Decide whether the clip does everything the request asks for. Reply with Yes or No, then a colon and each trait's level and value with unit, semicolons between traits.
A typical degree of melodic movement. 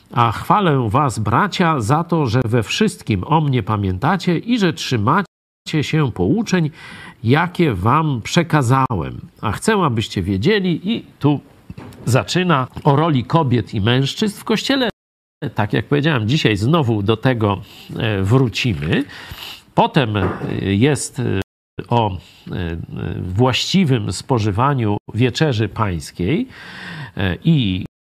No: wide, 6.7 semitones